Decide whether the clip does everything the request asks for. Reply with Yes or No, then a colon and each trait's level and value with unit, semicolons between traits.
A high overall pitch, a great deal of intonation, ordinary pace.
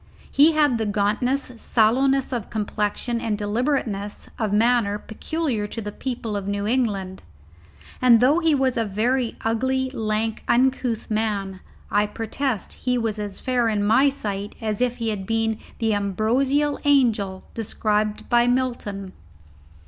No: high, 225 Hz; average, 3.5 semitones; average, 145 wpm